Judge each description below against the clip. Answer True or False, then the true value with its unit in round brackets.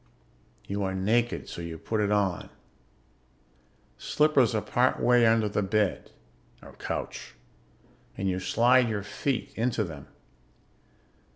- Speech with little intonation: False (3.7 semitones)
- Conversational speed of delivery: False (125 wpm)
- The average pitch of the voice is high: False (105 Hz)